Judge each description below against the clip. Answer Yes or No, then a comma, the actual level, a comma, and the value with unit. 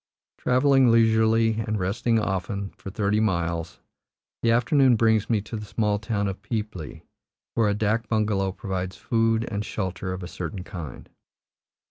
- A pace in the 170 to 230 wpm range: No, average, 150 wpm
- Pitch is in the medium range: No, low, 105 Hz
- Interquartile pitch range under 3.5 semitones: Yes, average, 2.9 semitones